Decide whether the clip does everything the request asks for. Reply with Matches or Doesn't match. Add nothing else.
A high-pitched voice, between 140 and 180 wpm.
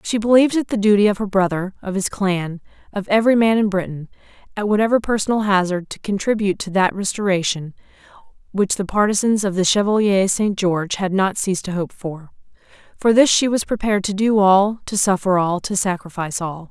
Doesn't match